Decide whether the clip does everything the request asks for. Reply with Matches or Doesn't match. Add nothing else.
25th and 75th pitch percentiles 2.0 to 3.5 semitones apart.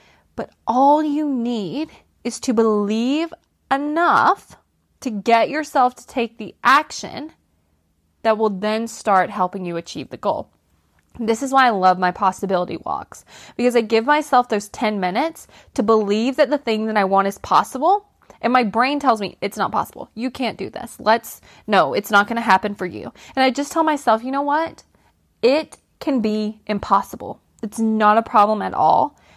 Doesn't match